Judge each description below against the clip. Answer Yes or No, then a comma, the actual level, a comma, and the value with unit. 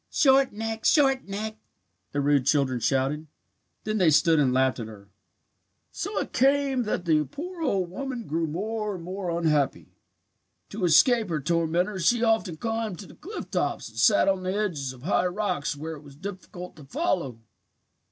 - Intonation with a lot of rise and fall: Yes, wide, 6.7 semitones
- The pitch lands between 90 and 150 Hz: No, medium, 180 Hz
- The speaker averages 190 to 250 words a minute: No, average, 175 wpm